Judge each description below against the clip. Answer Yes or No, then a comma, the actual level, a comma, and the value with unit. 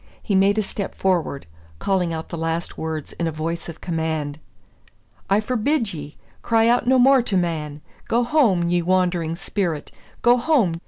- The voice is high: No, medium, 180 Hz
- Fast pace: No, average, 170 wpm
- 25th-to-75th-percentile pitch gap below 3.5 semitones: No, wide, 5.4 semitones